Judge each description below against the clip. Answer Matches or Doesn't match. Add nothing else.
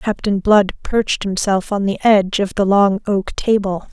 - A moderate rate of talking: Matches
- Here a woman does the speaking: Matches